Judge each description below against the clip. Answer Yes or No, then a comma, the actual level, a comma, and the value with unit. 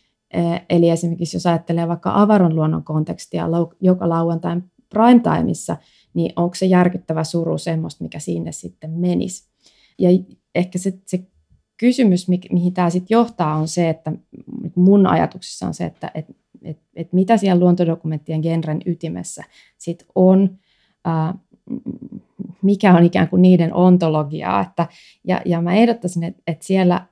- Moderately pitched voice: Yes, medium, 175 Hz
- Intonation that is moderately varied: No, narrow, 2.1 semitones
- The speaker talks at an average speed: Yes, average, 145 wpm